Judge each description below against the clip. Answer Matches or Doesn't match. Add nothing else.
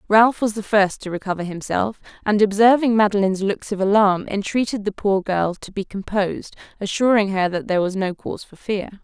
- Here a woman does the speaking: Matches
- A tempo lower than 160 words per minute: Doesn't match